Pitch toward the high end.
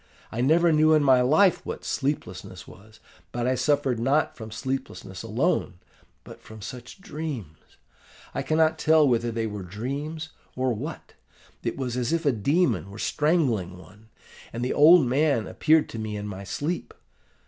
No: low, 125 Hz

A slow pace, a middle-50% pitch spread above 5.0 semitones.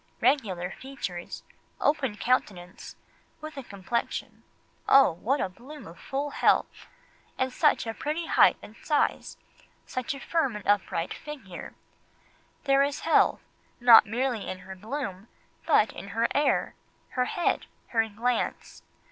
Yes: slow, 130 wpm; wide, 5.6 semitones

